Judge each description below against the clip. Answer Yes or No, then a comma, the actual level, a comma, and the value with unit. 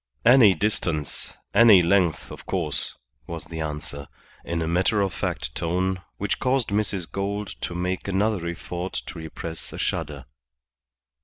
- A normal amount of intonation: Yes, average, 3.5 semitones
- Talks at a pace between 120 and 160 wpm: Yes, average, 145 wpm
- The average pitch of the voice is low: Yes, very low, 90 Hz